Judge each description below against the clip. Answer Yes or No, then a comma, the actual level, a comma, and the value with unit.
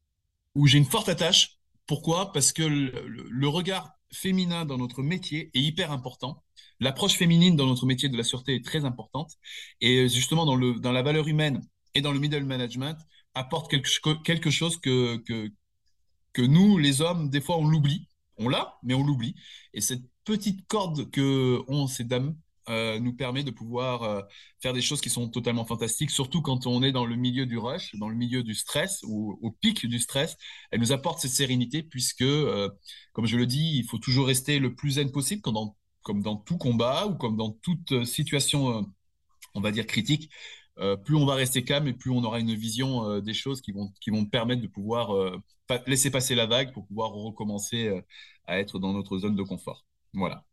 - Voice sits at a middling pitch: No, low, 130 Hz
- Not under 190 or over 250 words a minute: Yes, average, 210 wpm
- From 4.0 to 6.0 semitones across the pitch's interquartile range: Yes, average, 4.4 semitones